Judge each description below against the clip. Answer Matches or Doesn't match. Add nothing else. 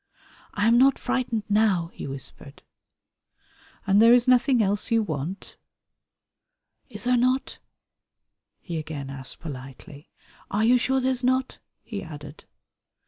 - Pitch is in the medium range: Doesn't match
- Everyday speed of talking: Doesn't match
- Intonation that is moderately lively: Doesn't match